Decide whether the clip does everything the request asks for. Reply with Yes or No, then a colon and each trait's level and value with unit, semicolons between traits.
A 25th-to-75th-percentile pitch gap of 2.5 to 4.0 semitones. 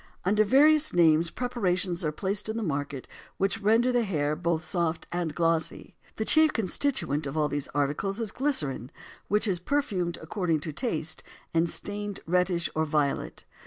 No: average, 5.3 semitones